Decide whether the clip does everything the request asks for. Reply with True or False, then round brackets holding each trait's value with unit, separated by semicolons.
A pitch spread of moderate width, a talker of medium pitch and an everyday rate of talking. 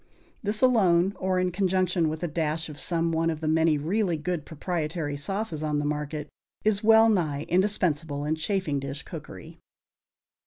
True (3.7 semitones; 165 Hz; 165 wpm)